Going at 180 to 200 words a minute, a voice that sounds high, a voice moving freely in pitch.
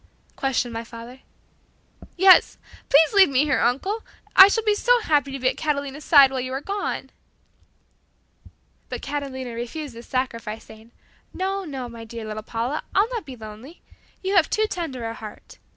No: average, 170 wpm; very high, 270 Hz; wide, 6.7 semitones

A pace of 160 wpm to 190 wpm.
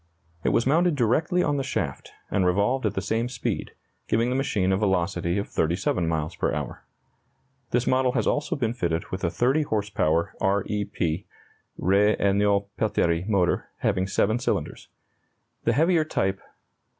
Yes: average, 170 wpm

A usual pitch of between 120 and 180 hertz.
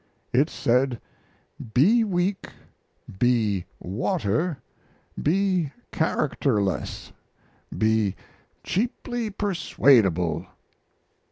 Yes: low, 135 Hz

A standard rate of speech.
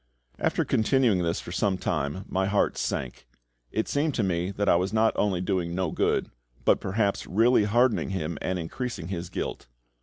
Yes: average, 180 wpm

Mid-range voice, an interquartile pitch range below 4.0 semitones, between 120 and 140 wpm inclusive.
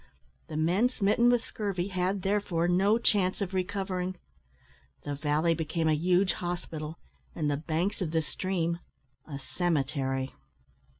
Yes: medium, 175 Hz; average, 3.5 semitones; slow, 135 wpm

